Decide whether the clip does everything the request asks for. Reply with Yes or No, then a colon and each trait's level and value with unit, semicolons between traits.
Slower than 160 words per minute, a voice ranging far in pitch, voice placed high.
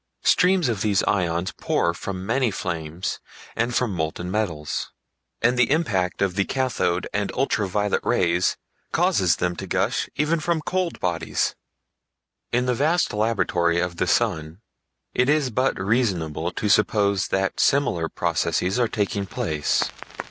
No: average, 145 wpm; wide, 5.9 semitones; low, 100 Hz